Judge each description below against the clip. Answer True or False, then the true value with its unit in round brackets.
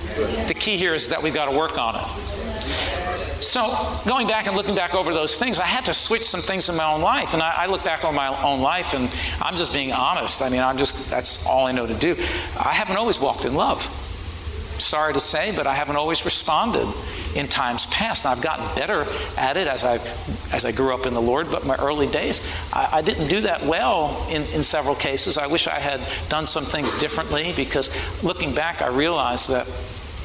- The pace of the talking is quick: True (225 wpm)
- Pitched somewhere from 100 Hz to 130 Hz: False (140 Hz)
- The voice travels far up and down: True (7.3 semitones)